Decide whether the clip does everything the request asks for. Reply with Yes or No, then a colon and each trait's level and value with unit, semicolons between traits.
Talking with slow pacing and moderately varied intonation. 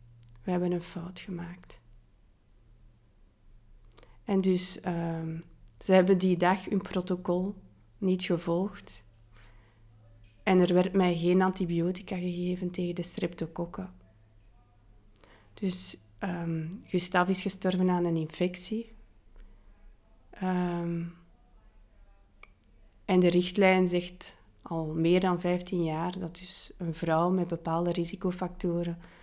No: slow, 105 wpm; wide, 8.5 semitones